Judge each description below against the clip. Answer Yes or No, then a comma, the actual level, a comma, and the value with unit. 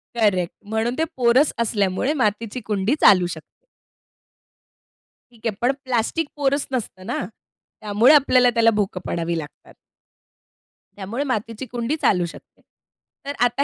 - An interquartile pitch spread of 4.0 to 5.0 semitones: Yes, average, 4.3 semitones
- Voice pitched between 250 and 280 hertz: No, high, 230 Hz